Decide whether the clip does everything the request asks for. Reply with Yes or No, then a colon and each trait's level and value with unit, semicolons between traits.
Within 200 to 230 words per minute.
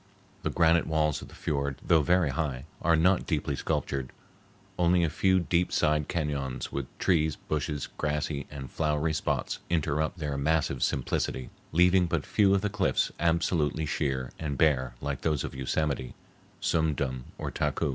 No: average, 160 wpm